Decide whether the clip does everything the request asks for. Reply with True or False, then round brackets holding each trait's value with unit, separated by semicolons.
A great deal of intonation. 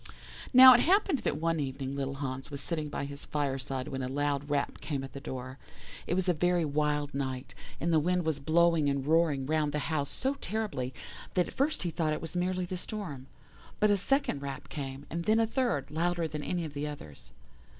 False (4.2 semitones)